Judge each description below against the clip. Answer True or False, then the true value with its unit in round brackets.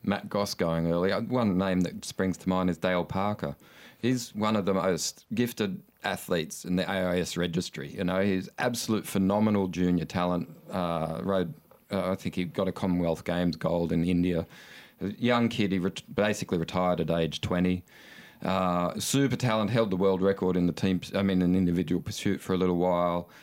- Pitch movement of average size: False (2.0 semitones)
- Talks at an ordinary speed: True (190 wpm)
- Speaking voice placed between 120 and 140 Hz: False (95 Hz)